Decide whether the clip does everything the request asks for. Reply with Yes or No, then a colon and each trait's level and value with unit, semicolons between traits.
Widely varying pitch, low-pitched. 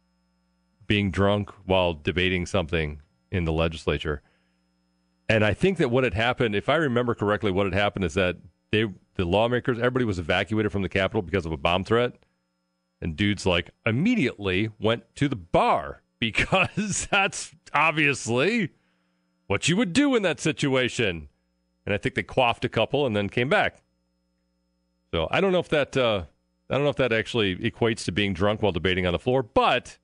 Yes: wide, 7.7 semitones; low, 100 Hz